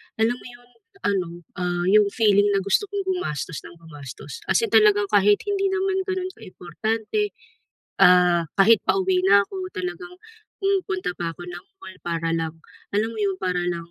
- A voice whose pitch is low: No, high, 205 Hz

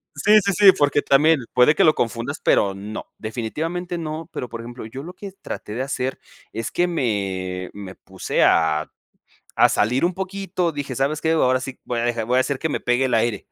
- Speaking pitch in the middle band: No, low, 130 Hz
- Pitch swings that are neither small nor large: No, wide, 6.1 semitones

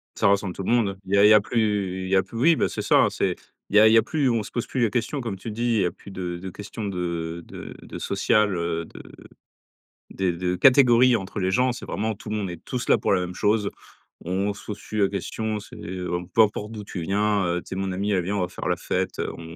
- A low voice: Yes, low, 100 Hz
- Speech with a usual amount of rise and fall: Yes, average, 3.0 semitones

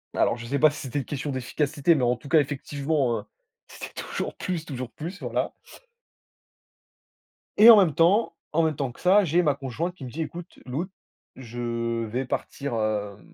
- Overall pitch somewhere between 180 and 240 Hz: No, medium, 140 Hz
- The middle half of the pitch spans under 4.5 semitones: No, average, 5.1 semitones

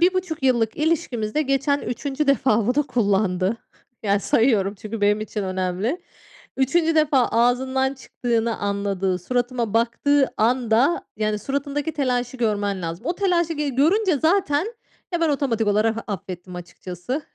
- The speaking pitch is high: Yes, high, 245 Hz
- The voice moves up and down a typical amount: No, wide, 5.7 semitones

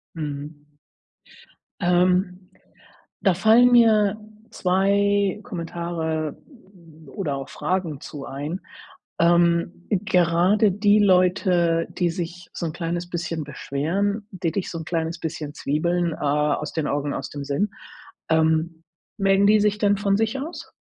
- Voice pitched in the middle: Yes, medium, 175 Hz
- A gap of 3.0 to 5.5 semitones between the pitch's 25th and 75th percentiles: Yes, average, 3.7 semitones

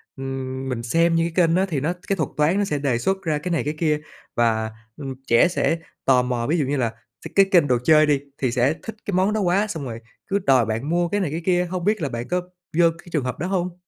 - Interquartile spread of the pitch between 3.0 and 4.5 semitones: No, wide, 5.4 semitones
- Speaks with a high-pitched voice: No, medium, 155 Hz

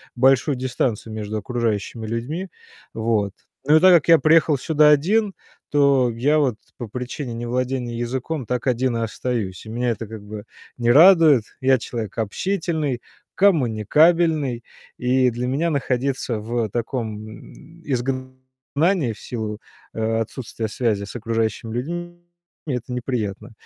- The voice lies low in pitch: Yes, low, 125 Hz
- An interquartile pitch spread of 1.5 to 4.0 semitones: No, average, 4.4 semitones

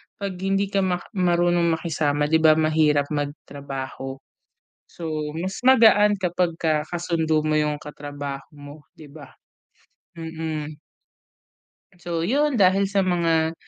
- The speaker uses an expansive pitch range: No, average, 3.3 semitones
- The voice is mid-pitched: Yes, medium, 160 Hz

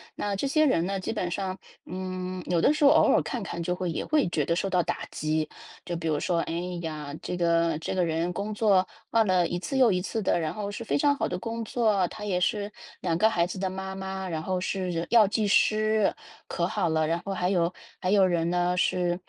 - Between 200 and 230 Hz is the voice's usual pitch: No, medium, 185 Hz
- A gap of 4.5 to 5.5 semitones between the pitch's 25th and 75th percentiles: No, average, 3.2 semitones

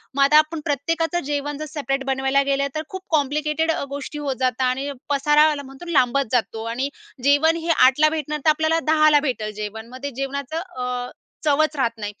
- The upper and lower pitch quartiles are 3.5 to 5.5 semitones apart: No, average, 2.7 semitones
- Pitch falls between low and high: No, very high, 285 Hz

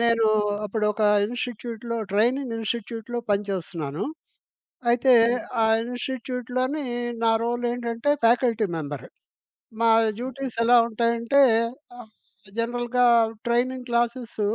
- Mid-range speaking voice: No, high, 235 Hz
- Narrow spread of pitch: Yes, narrow, 1.8 semitones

